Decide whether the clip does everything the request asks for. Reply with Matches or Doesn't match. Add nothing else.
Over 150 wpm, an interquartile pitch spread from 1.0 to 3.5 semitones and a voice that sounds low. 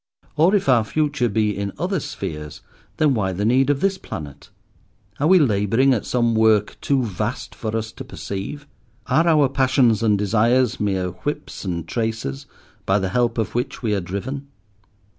Doesn't match